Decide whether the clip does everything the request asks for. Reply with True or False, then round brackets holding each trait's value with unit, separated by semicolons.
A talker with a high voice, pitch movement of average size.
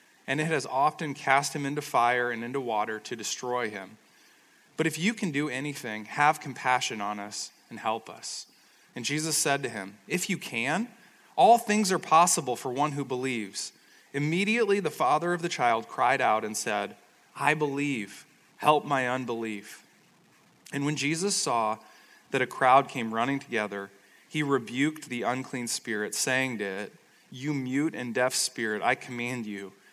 False (135 Hz; 4.3 semitones)